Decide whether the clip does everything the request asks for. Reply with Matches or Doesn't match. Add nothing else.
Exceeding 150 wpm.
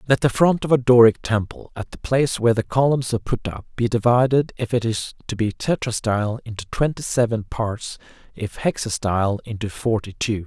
Matches